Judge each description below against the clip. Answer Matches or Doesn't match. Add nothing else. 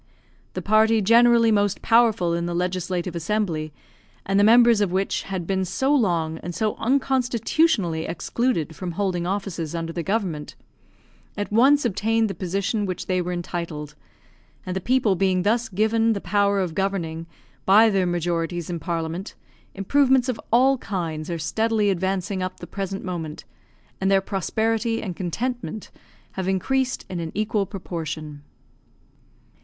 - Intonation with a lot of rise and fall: Doesn't match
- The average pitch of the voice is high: Matches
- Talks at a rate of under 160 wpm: Matches